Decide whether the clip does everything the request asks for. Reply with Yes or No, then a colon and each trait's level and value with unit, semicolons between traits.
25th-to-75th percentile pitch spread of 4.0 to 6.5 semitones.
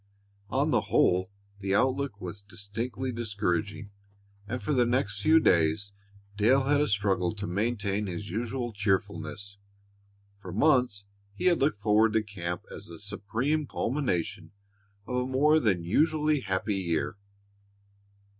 Yes: average, 4.6 semitones